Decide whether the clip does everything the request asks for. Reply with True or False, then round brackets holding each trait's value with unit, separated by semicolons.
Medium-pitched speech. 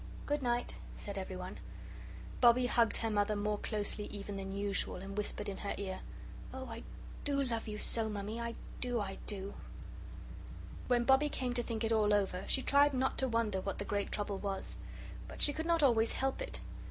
False (220 Hz)